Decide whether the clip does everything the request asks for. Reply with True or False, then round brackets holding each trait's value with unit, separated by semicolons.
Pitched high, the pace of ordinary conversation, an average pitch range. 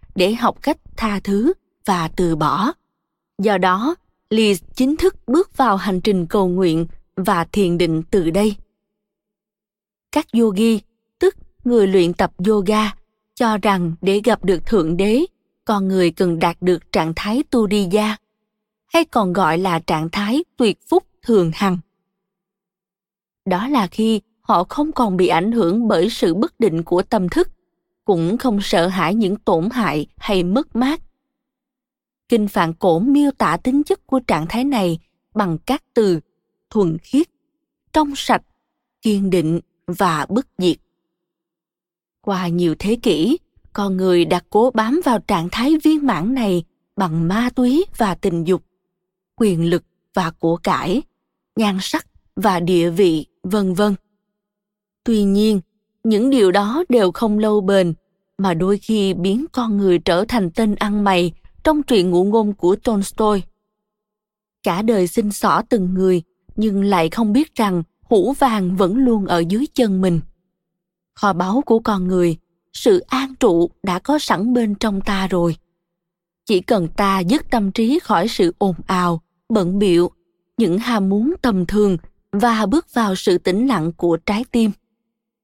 False (205 Hz; 160 wpm; 4.2 semitones)